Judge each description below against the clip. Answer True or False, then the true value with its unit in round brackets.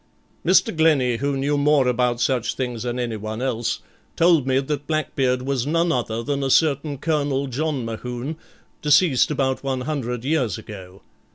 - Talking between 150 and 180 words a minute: True (160 wpm)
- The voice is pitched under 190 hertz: True (135 Hz)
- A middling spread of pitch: True (3.2 semitones)